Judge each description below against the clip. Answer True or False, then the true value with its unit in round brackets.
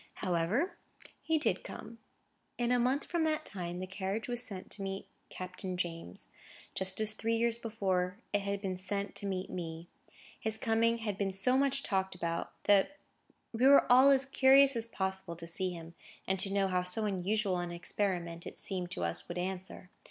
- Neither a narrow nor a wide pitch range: True (4.1 semitones)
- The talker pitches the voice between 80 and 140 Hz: False (195 Hz)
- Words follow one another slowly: False (190 wpm)